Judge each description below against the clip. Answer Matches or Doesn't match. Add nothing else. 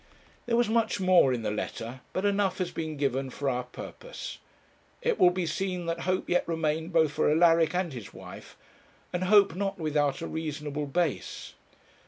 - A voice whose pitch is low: Doesn't match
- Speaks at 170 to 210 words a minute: Matches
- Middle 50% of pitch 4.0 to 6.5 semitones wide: Matches